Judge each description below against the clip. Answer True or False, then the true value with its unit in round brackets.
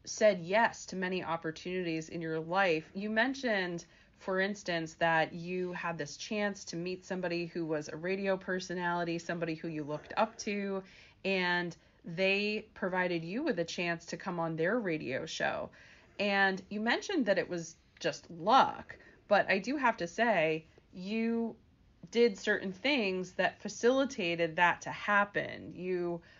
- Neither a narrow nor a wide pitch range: True (3.3 semitones)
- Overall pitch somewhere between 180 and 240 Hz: True (185 Hz)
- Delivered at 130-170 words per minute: True (155 wpm)